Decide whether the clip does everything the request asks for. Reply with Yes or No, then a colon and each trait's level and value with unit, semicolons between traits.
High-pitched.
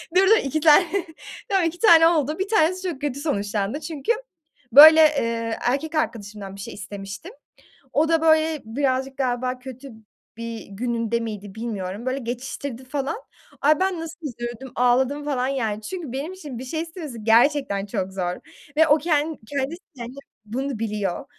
Yes: very high, 265 Hz